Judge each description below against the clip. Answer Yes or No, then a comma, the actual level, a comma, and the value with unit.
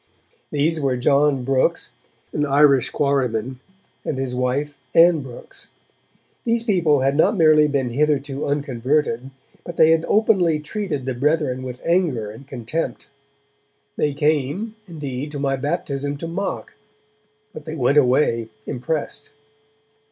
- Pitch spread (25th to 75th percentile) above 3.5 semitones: No, average, 3.1 semitones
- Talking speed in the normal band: No, slow, 130 wpm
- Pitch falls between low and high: Yes, medium, 145 Hz